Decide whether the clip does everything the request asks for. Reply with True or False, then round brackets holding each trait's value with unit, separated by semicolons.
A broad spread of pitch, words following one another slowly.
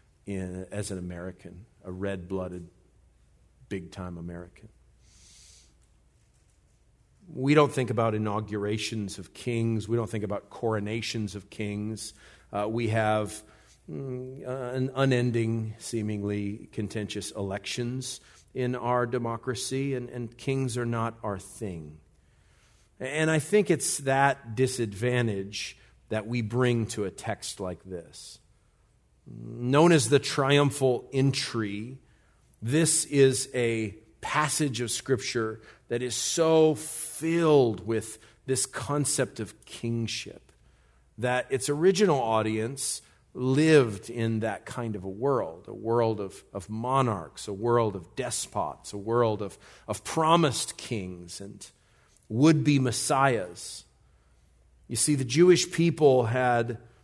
False (4.2 semitones; 120 wpm)